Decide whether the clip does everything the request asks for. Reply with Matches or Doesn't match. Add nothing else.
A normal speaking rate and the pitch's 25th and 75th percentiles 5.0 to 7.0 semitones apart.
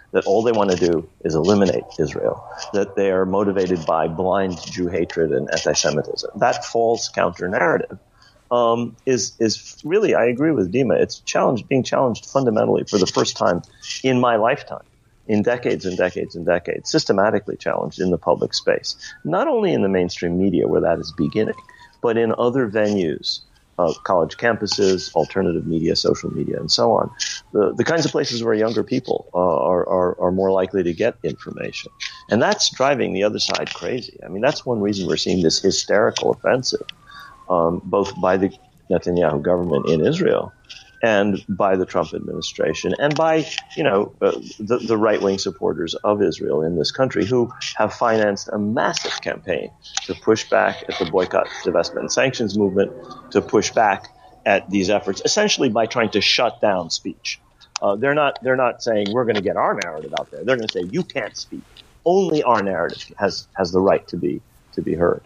Doesn't match